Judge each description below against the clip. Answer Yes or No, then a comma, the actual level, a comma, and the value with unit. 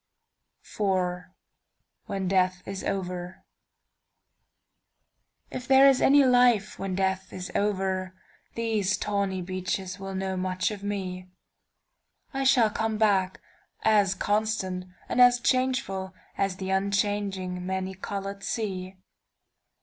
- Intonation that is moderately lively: No, narrow, 2.1 semitones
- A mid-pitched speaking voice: No, high, 195 Hz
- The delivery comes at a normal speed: No, slow, 100 wpm